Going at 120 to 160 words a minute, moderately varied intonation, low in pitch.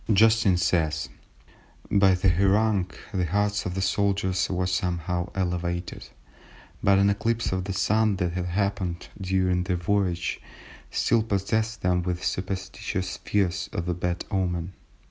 No: average, 140 wpm; narrow, 2.0 semitones; very low, 95 Hz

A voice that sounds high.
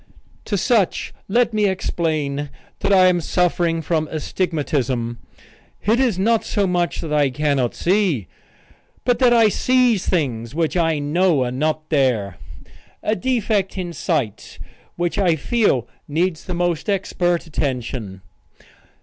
No: medium, 170 Hz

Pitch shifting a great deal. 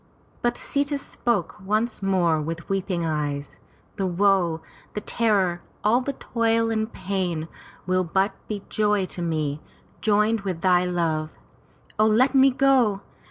No: average, 4.7 semitones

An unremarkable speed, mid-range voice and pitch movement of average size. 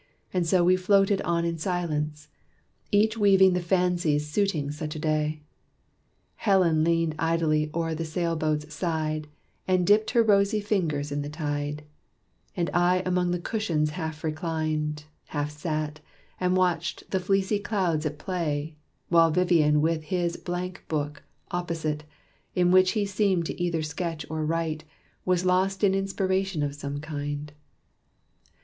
Yes: average, 145 wpm; medium, 165 Hz; average, 3.2 semitones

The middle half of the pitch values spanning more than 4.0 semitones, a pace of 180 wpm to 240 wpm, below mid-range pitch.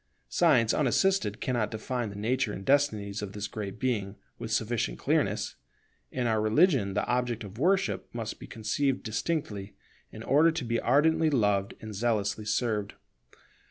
No: average, 4.4 semitones; average, 155 wpm; low, 115 Hz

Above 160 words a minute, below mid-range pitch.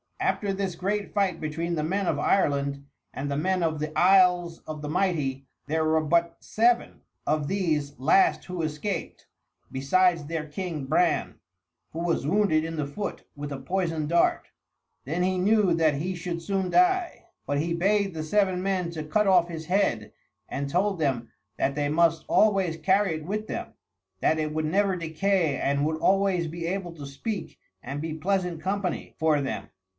No: average, 180 wpm; medium, 170 Hz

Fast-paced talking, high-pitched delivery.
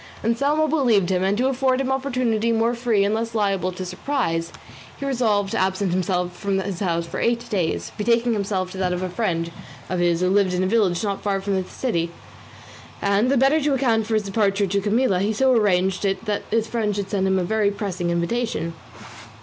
Yes: fast, 215 wpm; high, 205 Hz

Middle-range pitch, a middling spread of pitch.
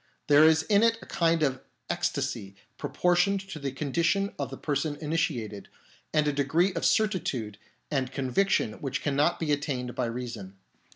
Yes: medium, 145 Hz; average, 4.6 semitones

